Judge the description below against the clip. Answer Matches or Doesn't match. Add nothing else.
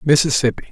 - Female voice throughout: Doesn't match